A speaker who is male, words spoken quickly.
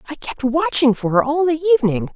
No: female; fast, 220 wpm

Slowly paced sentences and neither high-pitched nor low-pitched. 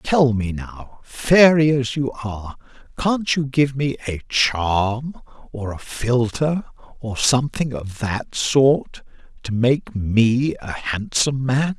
No: slow, 130 wpm; low, 125 Hz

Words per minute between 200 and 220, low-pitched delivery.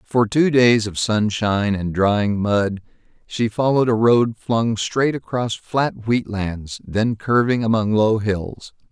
No: average, 150 wpm; low, 110 Hz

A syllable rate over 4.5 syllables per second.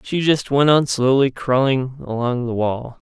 No: 4.2 syllables/s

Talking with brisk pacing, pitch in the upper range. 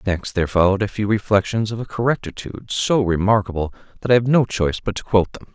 No: fast, 215 wpm; low, 105 Hz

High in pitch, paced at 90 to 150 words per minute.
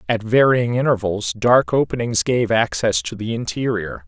No: low, 110 Hz; average, 145 wpm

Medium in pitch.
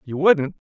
Yes: medium, 155 Hz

